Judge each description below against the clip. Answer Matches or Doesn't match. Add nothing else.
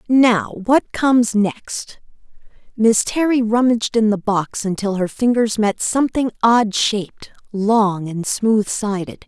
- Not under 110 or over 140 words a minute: Matches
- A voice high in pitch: Matches